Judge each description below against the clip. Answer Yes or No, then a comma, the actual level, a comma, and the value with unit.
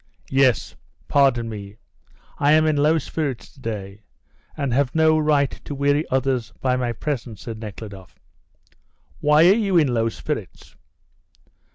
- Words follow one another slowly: No, average, 145 wpm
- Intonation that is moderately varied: Yes, average, 4.8 semitones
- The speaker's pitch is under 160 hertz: Yes, low, 135 Hz